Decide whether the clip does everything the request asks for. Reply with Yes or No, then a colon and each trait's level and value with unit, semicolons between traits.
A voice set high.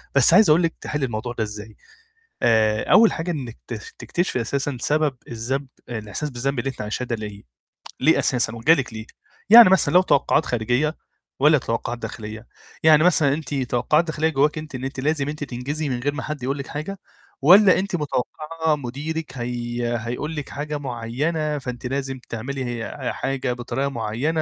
No: low, 135 Hz